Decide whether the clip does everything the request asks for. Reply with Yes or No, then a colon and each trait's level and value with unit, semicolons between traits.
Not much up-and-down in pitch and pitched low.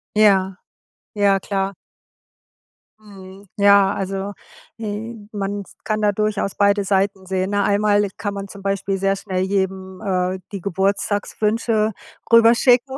No: narrow, 1.4 semitones; high, 200 Hz